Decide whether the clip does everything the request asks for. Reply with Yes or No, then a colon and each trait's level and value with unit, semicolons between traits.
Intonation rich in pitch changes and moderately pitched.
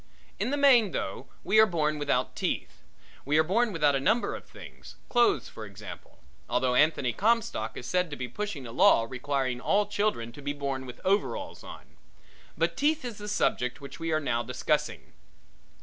Yes: wide, 8.5 semitones; medium, 150 Hz